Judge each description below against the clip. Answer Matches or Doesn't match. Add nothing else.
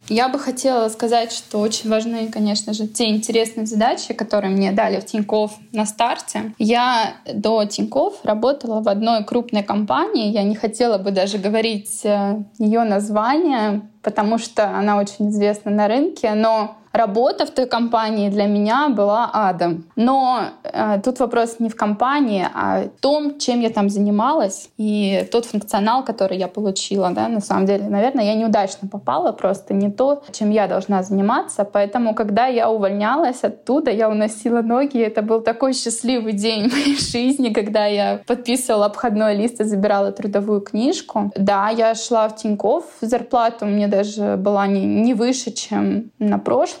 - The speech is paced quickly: Matches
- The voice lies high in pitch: Matches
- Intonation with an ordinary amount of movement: Doesn't match